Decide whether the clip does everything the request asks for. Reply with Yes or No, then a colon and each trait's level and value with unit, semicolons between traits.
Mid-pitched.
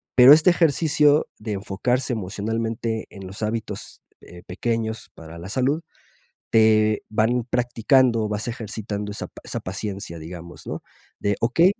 No: low, 110 Hz